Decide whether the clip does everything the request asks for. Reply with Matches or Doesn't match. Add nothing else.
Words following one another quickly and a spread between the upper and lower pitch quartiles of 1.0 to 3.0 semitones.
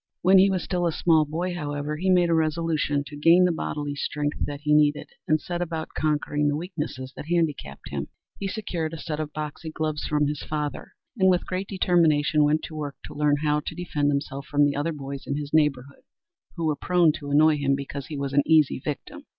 Matches